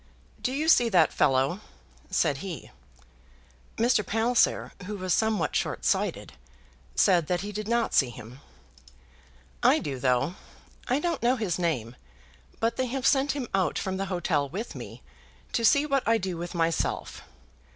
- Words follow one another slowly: No, average, 160 wpm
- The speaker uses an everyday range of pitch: No, wide, 6.2 semitones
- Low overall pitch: No, high, 195 Hz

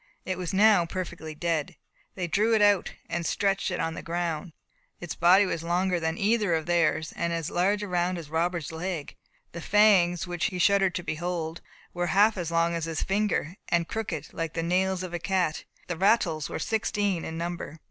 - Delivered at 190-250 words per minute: Yes, average, 200 wpm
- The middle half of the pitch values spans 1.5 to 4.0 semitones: Yes, narrow, 2.6 semitones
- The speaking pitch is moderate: Yes, medium, 175 Hz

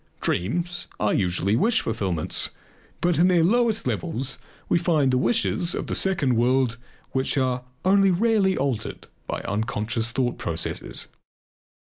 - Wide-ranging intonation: Yes, wide, 7.6 semitones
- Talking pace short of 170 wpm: Yes, slow, 135 wpm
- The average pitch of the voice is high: No, low, 135 Hz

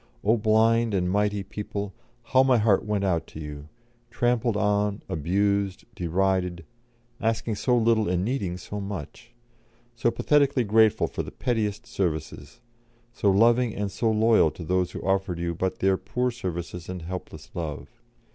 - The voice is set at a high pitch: No, low, 100 Hz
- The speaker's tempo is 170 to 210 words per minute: No, average, 155 wpm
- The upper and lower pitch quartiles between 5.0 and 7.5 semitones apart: No, average, 3.8 semitones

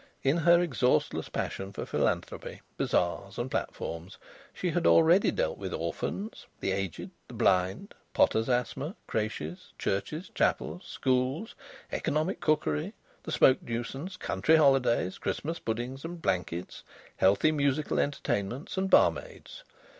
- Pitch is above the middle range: No, low, 135 Hz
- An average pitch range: No, wide, 8.8 semitones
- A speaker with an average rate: No, slow, 125 wpm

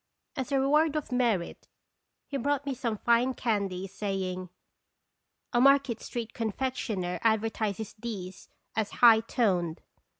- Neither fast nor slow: No, slow, 130 wpm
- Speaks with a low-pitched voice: No, high, 225 Hz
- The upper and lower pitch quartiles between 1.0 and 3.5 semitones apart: No, average, 4.7 semitones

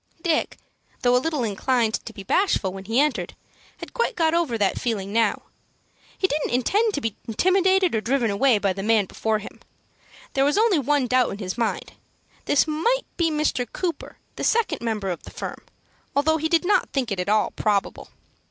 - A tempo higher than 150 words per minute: Yes, average, 195 wpm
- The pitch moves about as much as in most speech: No, wide, 7.0 semitones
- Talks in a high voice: Yes, very high, 255 Hz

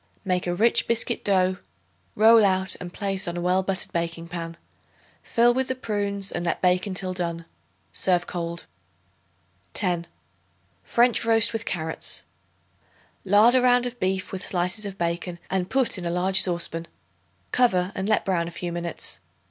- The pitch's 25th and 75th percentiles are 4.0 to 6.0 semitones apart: No, average, 3.3 semitones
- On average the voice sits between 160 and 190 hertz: Yes, medium, 185 Hz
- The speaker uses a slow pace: No, average, 165 wpm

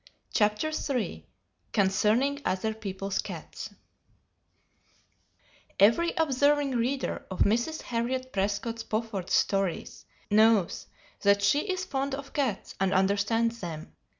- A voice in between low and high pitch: No, high, 225 Hz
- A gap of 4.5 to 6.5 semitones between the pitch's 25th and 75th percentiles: Yes, average, 5.1 semitones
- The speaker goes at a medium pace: No, slow, 105 wpm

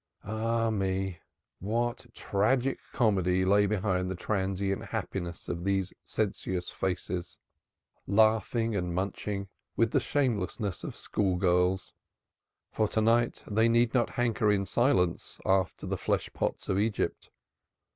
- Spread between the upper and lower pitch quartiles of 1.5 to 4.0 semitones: Yes, average, 3.2 semitones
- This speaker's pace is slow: Yes, slow, 125 wpm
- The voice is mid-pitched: No, low, 100 Hz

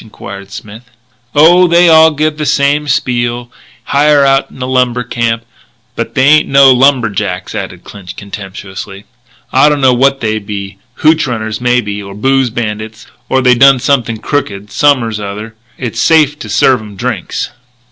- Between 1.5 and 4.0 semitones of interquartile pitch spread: No, average, 4.7 semitones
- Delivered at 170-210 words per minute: No, average, 160 wpm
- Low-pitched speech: Yes, low, 125 Hz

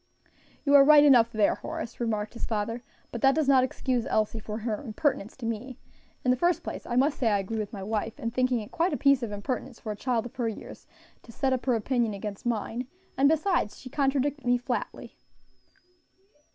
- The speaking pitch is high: Yes, high, 245 Hz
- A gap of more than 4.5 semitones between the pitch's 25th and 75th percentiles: No, average, 3.6 semitones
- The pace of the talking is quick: Yes, fast, 215 wpm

